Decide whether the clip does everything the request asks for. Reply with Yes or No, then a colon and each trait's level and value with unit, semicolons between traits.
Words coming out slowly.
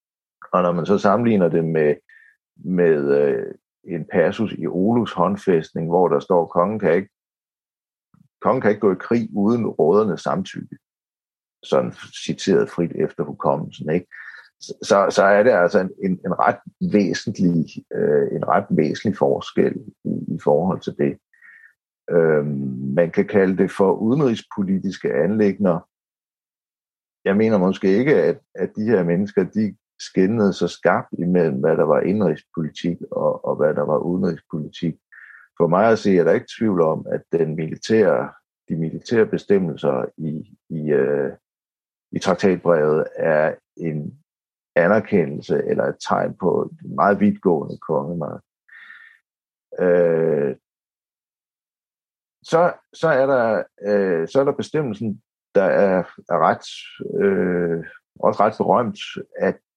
Yes: slow, 130 wpm